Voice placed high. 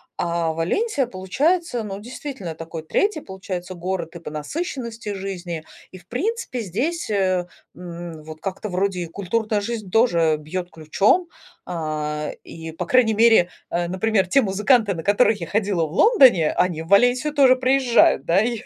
Yes: high, 195 Hz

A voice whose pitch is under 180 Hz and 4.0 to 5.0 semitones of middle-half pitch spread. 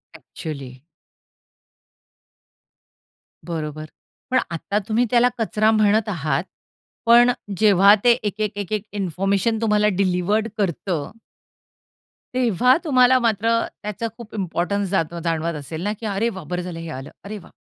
No: high, 200 Hz; average, 4.4 semitones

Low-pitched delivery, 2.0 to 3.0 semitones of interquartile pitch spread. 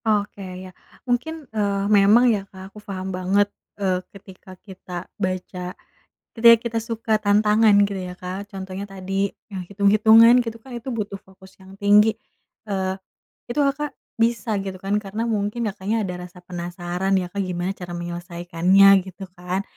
No: high, 195 Hz; narrow, 2.5 semitones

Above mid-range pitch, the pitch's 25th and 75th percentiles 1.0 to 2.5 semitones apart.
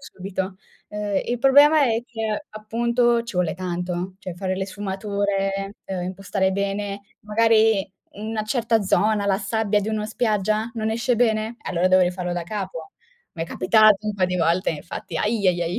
No: high, 205 Hz; average, 2.9 semitones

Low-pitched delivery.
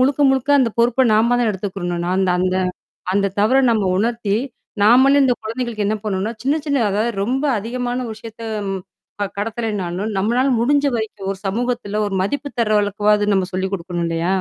No: high, 215 Hz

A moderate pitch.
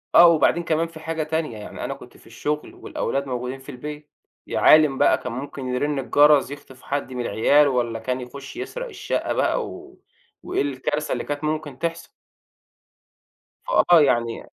Yes: medium, 145 Hz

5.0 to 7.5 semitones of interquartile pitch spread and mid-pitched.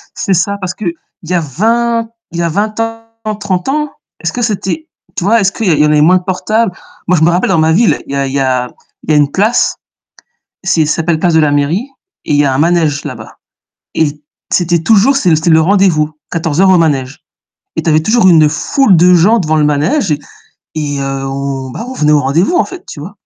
Yes: average, 5.3 semitones; medium, 170 Hz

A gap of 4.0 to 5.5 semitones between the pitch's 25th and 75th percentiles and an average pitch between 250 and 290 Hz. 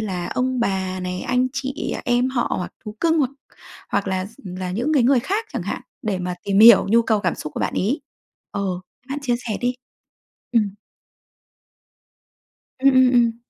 No: average, 5.0 semitones; high, 235 Hz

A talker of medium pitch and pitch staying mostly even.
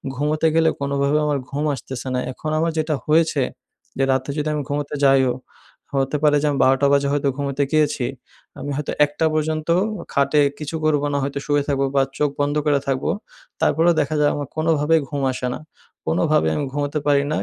Yes: medium, 145 Hz; narrow, 1.6 semitones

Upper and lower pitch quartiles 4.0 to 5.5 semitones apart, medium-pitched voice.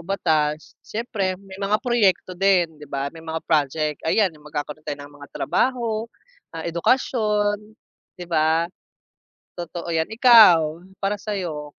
Yes: average, 5.0 semitones; medium, 175 Hz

